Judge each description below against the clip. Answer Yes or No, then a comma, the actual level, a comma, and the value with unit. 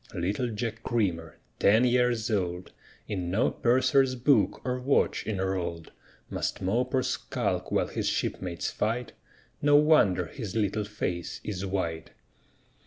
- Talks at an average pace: No, slow, 130 wpm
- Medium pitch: No, low, 105 Hz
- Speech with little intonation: No, average, 5.1 semitones